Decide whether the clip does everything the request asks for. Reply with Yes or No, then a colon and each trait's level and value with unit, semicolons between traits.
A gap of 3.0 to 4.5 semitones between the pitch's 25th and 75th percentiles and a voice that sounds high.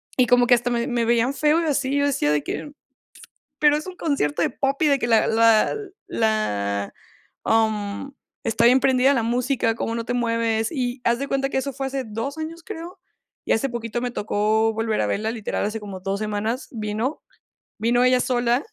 Yes: average, 3.5 semitones; high, 235 Hz